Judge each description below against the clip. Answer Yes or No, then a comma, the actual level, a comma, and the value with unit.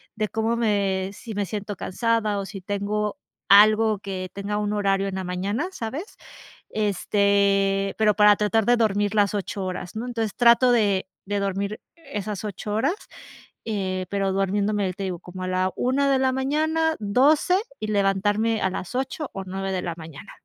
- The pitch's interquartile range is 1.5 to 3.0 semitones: Yes, narrow, 2.4 semitones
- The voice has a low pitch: No, high, 205 Hz